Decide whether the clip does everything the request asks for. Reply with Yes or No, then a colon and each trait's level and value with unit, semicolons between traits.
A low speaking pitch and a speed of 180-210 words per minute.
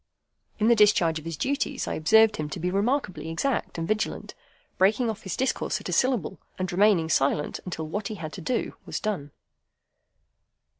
No: high, 195 Hz; average, 185 wpm